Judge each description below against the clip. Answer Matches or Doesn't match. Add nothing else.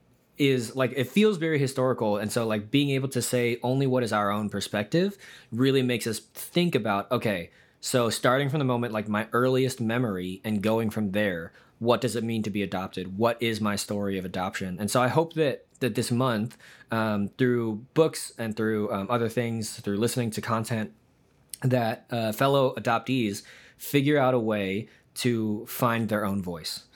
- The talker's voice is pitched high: Doesn't match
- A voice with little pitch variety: Doesn't match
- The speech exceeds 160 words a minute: Matches